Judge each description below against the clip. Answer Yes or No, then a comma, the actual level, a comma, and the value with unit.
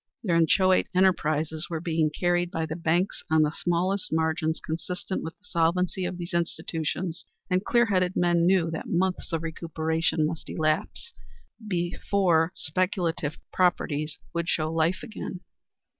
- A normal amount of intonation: No, narrow, 2.2 semitones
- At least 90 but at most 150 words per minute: Yes, average, 145 wpm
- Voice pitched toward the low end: No, medium, 170 Hz